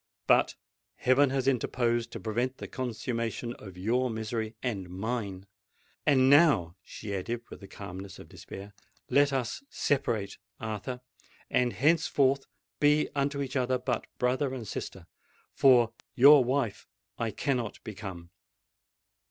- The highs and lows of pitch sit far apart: No, average, 3.9 semitones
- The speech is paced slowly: Yes, slow, 120 wpm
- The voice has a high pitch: No, low, 120 Hz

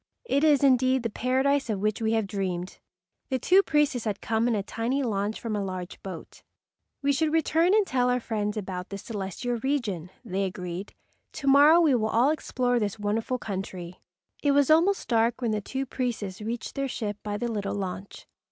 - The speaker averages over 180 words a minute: Yes, average, 195 wpm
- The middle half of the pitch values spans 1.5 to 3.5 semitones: No, average, 5.1 semitones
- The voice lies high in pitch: Yes, high, 230 Hz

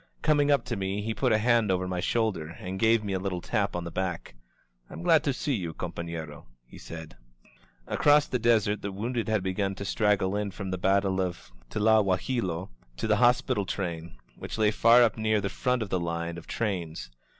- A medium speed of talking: No, fast, 215 wpm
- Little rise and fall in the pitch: No, average, 3.7 semitones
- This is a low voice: Yes, low, 100 Hz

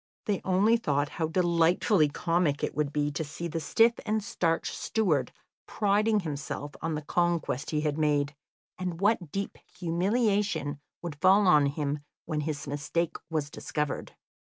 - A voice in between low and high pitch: Yes, medium, 165 Hz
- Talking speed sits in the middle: Yes, average, 155 wpm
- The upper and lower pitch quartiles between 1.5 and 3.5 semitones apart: No, average, 4.3 semitones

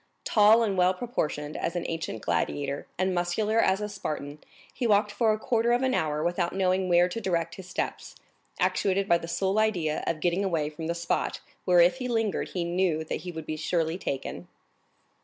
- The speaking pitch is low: No, medium, 180 Hz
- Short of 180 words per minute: No, average, 200 wpm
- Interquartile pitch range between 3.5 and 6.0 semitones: Yes, average, 3.8 semitones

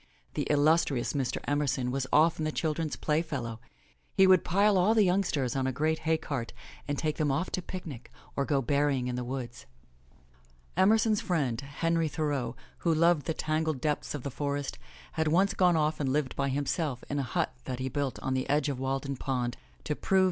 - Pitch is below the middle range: No, medium, 145 Hz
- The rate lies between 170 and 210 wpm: Yes, average, 195 wpm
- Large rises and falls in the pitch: No, average, 3.4 semitones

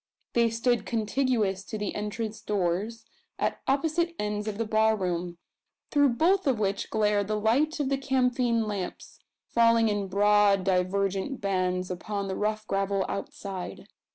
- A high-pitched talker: Yes, high, 210 Hz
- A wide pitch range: No, average, 3.0 semitones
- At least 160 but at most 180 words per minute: No, average, 150 wpm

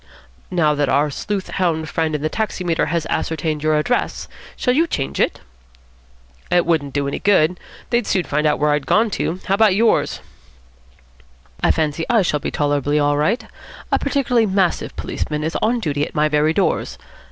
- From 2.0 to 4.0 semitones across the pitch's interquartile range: No, average, 4.9 semitones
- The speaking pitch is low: No, medium, 160 Hz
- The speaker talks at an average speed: Yes, average, 175 wpm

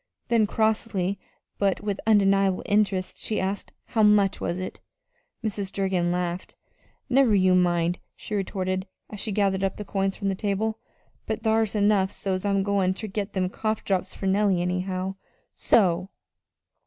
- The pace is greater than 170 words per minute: No, average, 155 wpm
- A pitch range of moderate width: No, narrow, 1.9 semitones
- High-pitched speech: Yes, high, 195 Hz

